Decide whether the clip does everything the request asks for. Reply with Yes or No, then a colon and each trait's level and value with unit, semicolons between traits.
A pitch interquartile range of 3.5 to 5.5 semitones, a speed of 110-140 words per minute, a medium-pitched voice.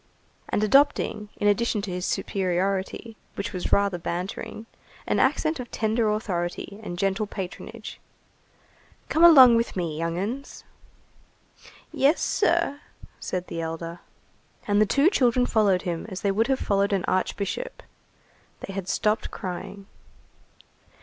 No: average, 4.1 semitones; slow, 135 wpm; high, 200 Hz